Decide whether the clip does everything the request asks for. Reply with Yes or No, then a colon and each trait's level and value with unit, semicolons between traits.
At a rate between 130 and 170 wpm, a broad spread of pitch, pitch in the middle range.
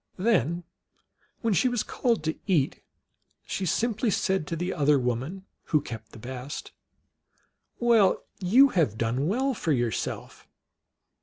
Yes: average, 140 wpm; wide, 8.4 semitones; medium, 175 Hz